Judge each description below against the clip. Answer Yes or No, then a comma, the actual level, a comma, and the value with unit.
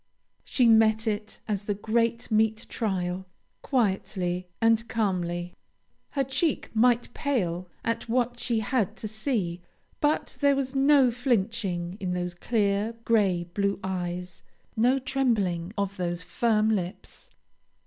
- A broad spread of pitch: No, average, 4.5 semitones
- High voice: Yes, high, 215 Hz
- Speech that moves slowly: Yes, slow, 130 wpm